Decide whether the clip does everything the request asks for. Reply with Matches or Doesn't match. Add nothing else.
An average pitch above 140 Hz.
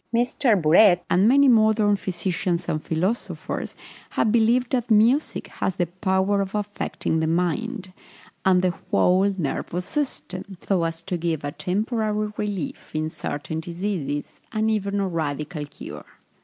Matches